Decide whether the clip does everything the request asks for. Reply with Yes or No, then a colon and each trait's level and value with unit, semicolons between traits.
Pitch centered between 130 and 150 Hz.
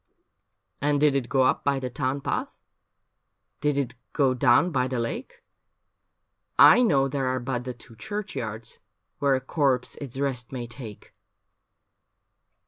Yes: low, 135 Hz